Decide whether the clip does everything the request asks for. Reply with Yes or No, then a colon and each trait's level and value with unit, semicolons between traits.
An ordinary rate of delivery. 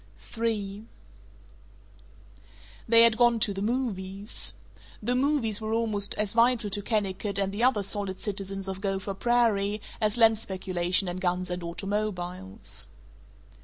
No: slow, 130 wpm